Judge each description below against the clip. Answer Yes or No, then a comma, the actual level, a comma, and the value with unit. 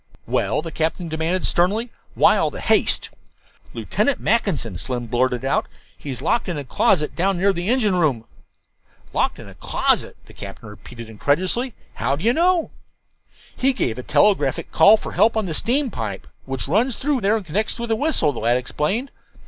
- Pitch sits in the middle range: Yes, medium, 180 Hz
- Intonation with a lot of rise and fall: Yes, wide, 9.0 semitones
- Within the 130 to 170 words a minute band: No, average, 180 wpm